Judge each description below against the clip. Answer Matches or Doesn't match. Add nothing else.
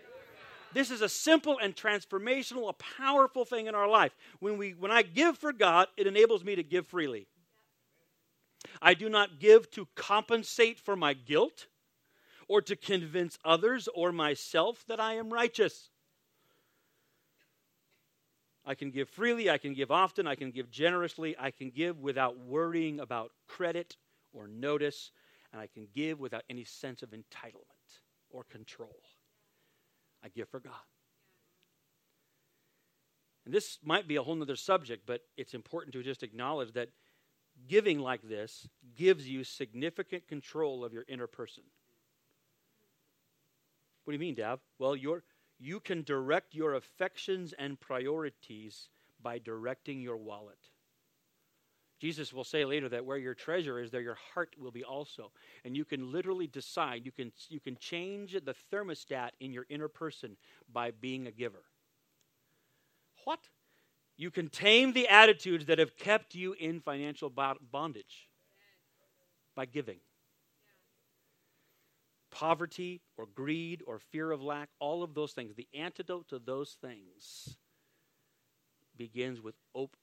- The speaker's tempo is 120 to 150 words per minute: Matches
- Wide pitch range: Matches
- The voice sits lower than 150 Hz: Doesn't match